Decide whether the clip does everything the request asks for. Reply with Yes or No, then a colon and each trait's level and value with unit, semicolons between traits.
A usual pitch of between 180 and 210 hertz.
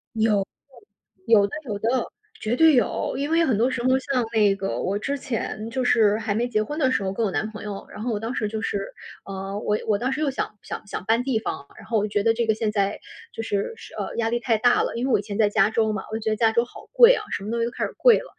No: high, 225 Hz